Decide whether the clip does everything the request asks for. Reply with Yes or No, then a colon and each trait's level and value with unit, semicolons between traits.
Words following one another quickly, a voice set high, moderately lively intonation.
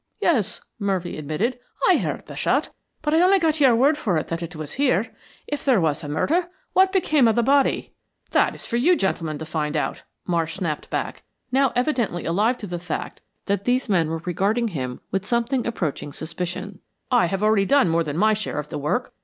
No: fast, 210 wpm; high, 205 Hz; wide, 7.4 semitones